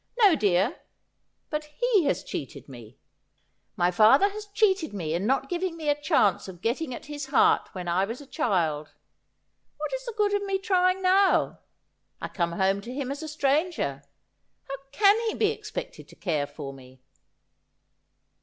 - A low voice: No, very high, 275 Hz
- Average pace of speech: Yes, average, 175 wpm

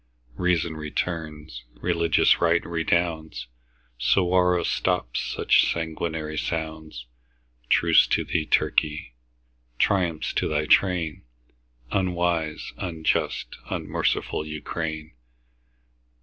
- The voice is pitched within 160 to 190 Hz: No, very low, 80 Hz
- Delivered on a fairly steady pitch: Yes, narrow, 2.0 semitones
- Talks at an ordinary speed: No, slow, 80 wpm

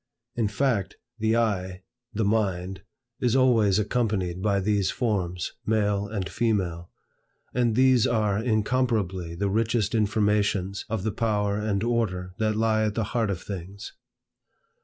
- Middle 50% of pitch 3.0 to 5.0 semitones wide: No, narrow, 2.6 semitones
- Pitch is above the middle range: No, low, 105 Hz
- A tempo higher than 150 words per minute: No, average, 140 wpm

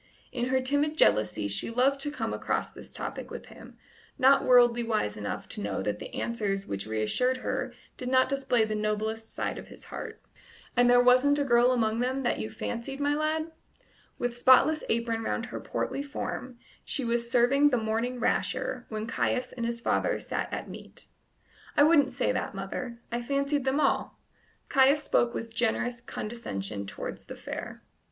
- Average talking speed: Yes, average, 180 wpm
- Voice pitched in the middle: No, high, 245 Hz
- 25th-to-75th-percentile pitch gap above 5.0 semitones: No, average, 3.2 semitones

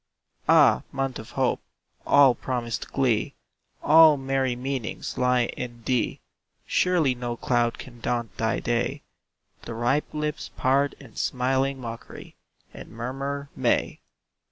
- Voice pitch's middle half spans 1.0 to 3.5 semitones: Yes, narrow, 2.5 semitones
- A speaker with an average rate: No, slow, 125 wpm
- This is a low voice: Yes, low, 130 Hz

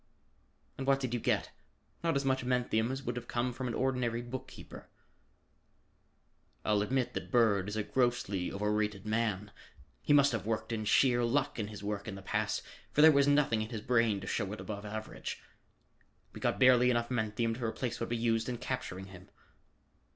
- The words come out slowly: No, average, 190 wpm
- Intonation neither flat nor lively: Yes, average, 3.1 semitones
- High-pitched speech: No, low, 115 Hz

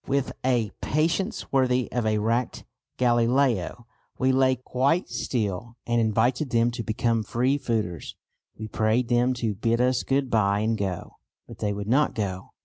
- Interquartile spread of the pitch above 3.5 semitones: No, average, 2.9 semitones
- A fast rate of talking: No, average, 160 wpm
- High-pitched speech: No, low, 120 Hz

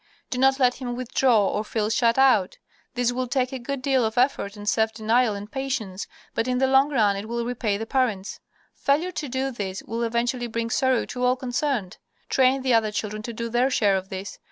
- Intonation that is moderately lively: Yes, average, 3.2 semitones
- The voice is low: No, high, 240 Hz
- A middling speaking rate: No, fast, 220 wpm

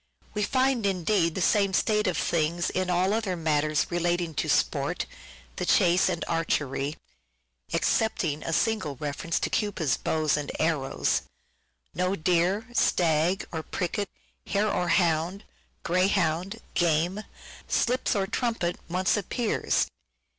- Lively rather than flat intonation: No, average, 3.9 semitones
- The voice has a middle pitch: Yes, medium, 180 Hz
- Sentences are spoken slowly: Yes, slow, 125 wpm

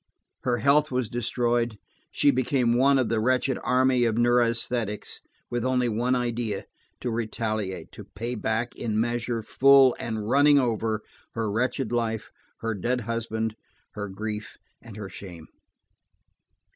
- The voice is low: Yes, low, 120 Hz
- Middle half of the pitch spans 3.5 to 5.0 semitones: No, narrow, 2.4 semitones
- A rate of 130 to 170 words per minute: Yes, average, 140 wpm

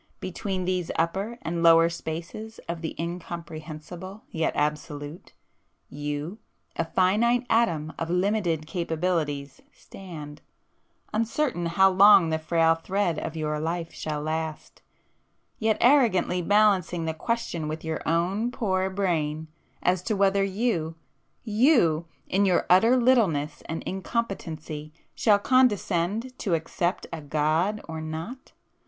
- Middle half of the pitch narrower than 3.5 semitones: No, average, 4.1 semitones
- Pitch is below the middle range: No, medium, 175 Hz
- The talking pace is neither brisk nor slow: No, slow, 120 wpm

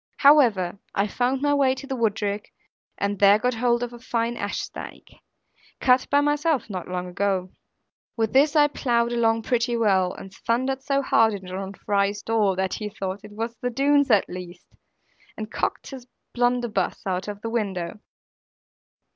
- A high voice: Yes, high, 225 Hz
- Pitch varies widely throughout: No, average, 4.1 semitones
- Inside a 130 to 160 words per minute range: No, average, 170 wpm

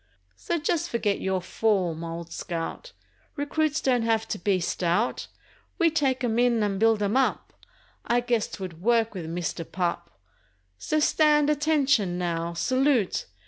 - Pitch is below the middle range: No, high, 225 Hz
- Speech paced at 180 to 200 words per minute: No, average, 140 wpm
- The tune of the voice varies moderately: No, wide, 7.2 semitones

